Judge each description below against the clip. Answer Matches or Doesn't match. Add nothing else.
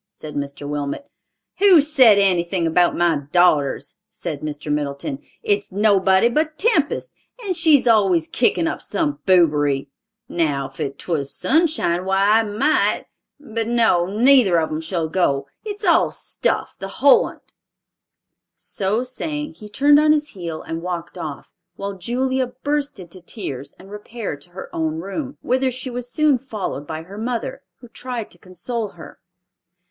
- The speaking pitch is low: Doesn't match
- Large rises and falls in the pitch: Matches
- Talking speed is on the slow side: Doesn't match